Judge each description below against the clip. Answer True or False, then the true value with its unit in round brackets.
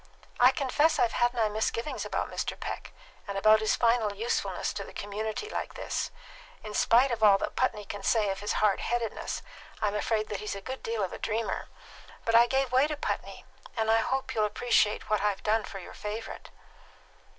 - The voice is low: False (220 Hz)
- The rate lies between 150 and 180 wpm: False (200 wpm)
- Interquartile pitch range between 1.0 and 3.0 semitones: True (2.5 semitones)